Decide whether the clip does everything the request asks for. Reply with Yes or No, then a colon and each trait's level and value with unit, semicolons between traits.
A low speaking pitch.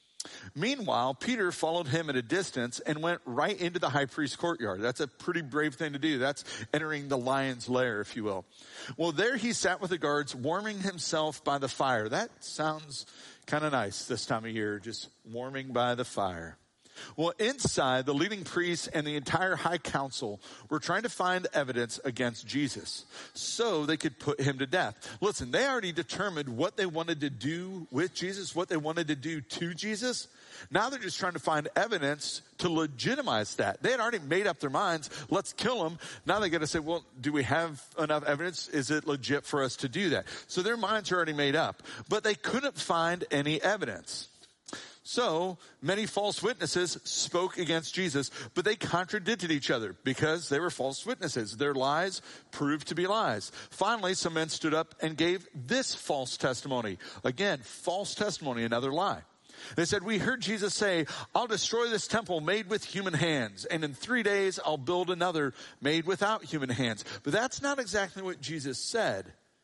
No: medium, 160 Hz